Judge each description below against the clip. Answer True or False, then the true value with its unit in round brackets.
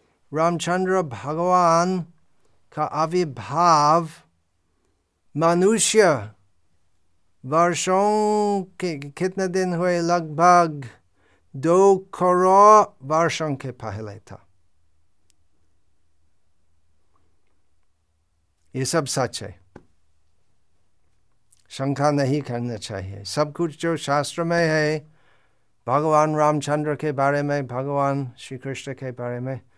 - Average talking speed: False (85 wpm)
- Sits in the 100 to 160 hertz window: True (135 Hz)